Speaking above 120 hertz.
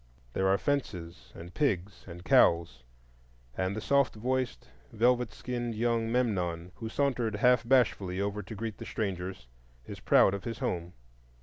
No: low, 110 Hz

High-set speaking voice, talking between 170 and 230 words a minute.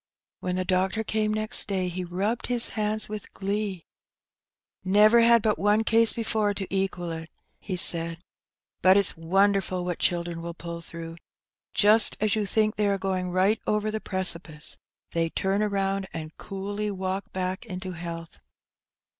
No: high, 195 Hz; average, 160 wpm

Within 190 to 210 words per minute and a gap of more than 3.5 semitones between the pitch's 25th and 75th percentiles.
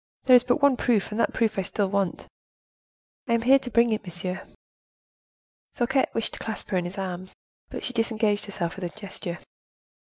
Yes: average, 195 wpm; average, 4.0 semitones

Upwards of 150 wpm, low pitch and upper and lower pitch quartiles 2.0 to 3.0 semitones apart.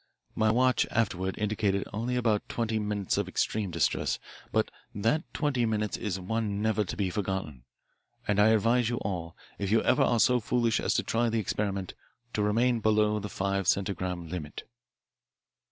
Yes: average, 170 wpm; low, 105 Hz; average, 2.7 semitones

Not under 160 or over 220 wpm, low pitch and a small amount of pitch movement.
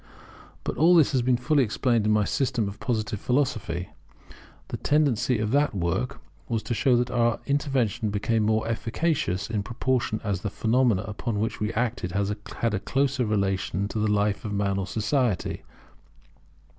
No: average, 170 wpm; low, 110 Hz; average, 3.6 semitones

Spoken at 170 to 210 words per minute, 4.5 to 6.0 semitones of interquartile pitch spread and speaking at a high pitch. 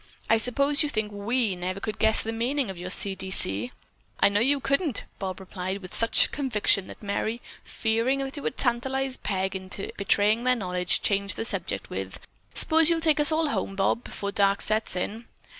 Yes: average, 190 wpm; average, 5.2 semitones; high, 220 Hz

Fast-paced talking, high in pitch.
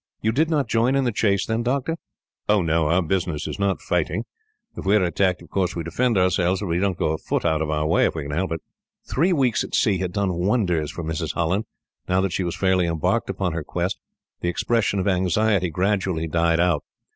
No: fast, 230 wpm; very low, 95 Hz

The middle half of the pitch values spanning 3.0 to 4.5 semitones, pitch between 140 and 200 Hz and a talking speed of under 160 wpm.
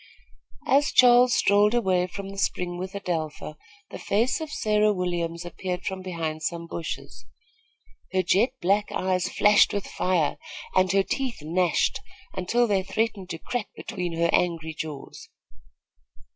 Yes: average, 3.4 semitones; medium, 185 Hz; average, 145 wpm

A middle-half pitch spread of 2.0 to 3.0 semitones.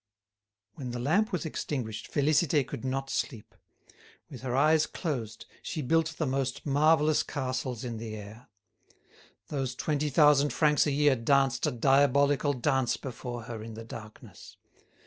No: average, 3.5 semitones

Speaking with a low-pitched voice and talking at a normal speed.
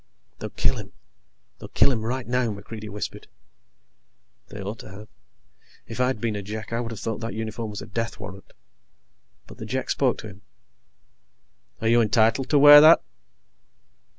Yes: low, 110 Hz; average, 175 wpm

